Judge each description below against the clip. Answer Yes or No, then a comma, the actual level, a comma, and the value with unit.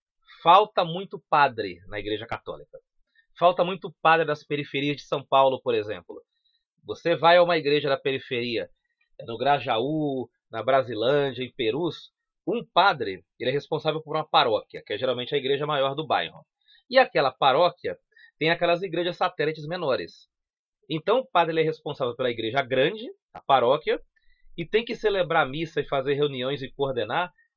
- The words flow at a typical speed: Yes, average, 160 wpm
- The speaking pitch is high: No, medium, 170 Hz